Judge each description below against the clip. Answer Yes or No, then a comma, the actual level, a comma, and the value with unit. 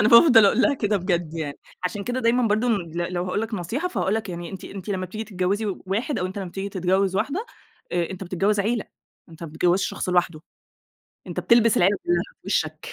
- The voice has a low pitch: No, high, 195 Hz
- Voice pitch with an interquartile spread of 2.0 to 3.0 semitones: No, average, 3.8 semitones